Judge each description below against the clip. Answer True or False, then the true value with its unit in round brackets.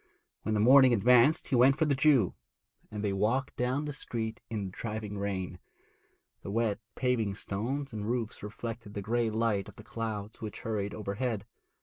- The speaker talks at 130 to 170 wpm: False (180 wpm)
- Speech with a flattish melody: False (3.2 semitones)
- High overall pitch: False (110 Hz)